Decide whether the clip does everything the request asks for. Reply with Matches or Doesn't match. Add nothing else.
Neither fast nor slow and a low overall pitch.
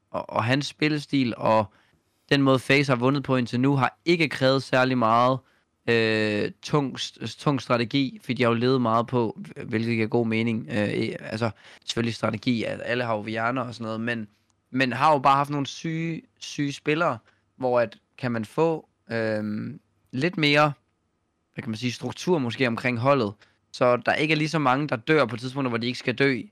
Matches